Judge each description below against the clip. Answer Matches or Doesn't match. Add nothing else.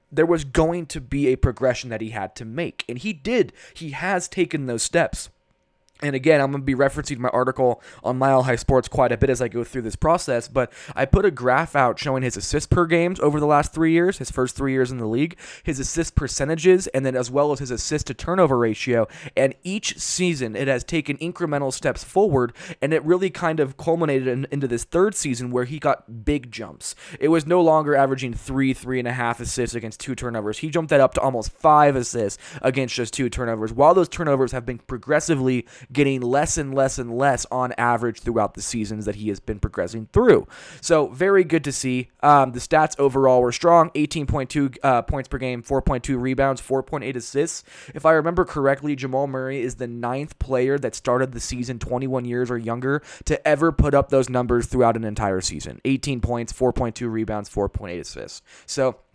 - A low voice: Matches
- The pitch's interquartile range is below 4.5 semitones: Matches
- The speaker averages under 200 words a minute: Doesn't match